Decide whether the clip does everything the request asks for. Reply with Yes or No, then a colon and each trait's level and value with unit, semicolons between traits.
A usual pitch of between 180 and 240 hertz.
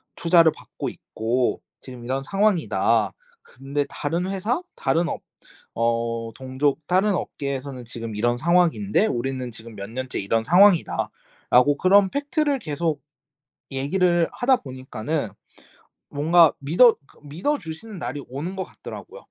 No: medium, 145 Hz